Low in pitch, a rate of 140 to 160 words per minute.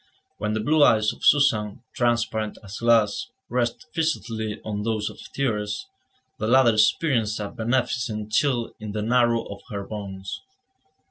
Yes: low, 110 Hz; average, 145 wpm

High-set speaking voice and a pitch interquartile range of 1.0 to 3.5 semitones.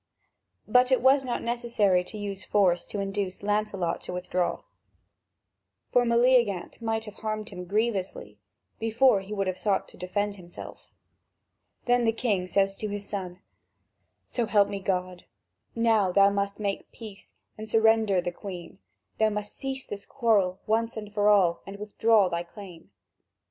Yes: high, 205 Hz; average, 2.8 semitones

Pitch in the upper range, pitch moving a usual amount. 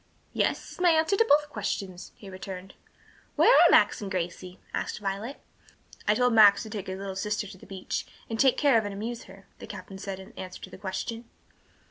Yes: high, 205 Hz; average, 3.4 semitones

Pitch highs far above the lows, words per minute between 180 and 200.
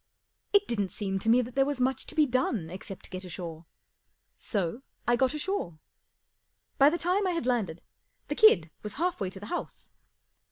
Yes: wide, 7.7 semitones; average, 190 wpm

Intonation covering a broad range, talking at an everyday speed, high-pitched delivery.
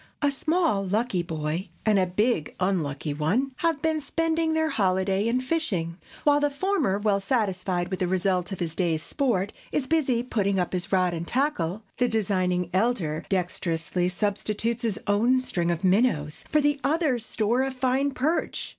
Yes: wide, 6.5 semitones; average, 165 wpm; high, 205 Hz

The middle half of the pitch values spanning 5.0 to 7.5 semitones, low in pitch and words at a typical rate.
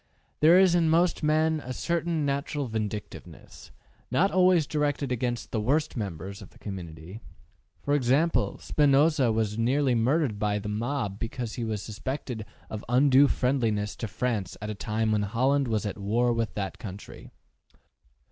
Yes: average, 5.3 semitones; low, 120 Hz; average, 160 wpm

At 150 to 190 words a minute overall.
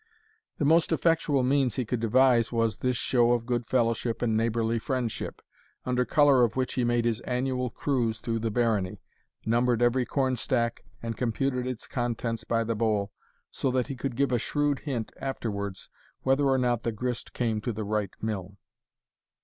Yes: average, 180 wpm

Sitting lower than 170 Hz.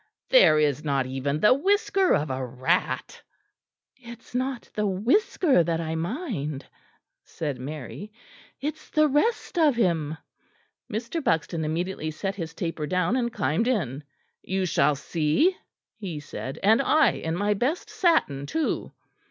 No: medium, 180 Hz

